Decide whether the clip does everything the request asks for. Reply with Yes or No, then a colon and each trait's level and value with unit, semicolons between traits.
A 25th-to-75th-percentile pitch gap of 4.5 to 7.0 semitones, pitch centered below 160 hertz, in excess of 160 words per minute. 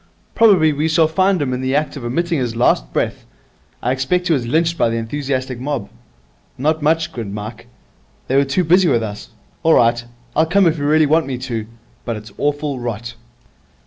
Yes: average, 5.1 semitones; medium, 140 Hz; average, 200 wpm